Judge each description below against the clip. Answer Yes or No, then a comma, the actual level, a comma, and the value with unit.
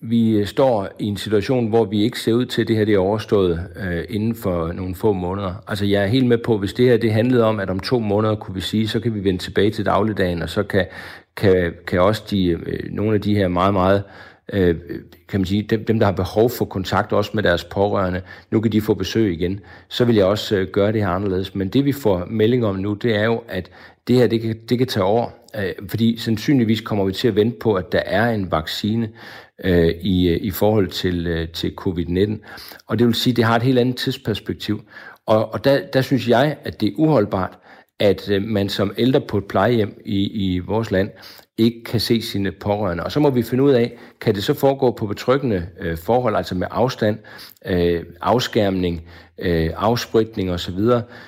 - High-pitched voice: No, low, 105 Hz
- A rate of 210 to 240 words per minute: Yes, average, 220 wpm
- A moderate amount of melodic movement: Yes, average, 3.4 semitones